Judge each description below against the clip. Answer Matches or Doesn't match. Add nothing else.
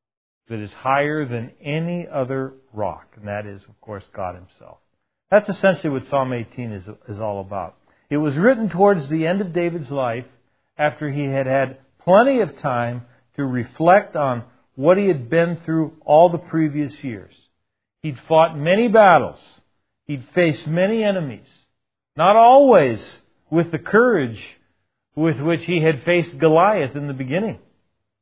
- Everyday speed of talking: Matches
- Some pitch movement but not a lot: Doesn't match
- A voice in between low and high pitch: Matches